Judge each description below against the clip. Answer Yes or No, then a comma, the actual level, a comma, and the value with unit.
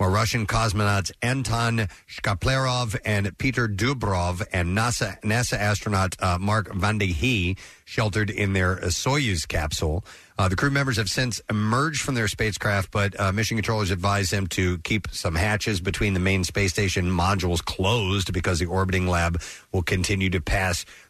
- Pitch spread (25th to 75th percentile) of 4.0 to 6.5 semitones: No, average, 3.1 semitones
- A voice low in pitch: Yes, low, 100 Hz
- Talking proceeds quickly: No, average, 160 wpm